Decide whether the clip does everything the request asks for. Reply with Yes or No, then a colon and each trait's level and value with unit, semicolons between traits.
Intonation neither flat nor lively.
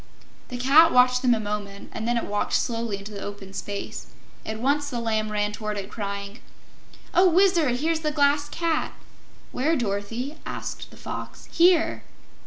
No: wide, 6.1 semitones